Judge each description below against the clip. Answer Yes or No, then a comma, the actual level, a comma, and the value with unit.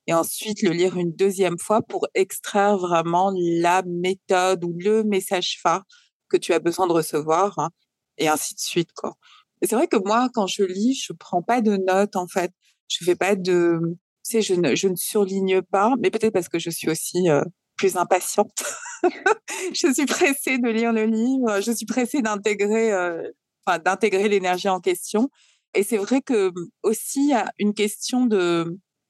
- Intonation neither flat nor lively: Yes, average, 3.9 semitones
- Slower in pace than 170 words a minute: No, average, 190 wpm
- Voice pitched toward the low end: No, high, 195 Hz